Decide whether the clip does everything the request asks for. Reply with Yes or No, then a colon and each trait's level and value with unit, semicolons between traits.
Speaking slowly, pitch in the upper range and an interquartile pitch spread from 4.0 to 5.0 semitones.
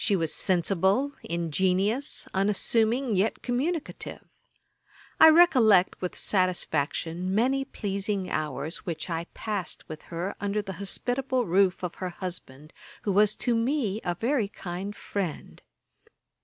Yes: slow, 125 wpm; high, 195 Hz; average, 4.4 semitones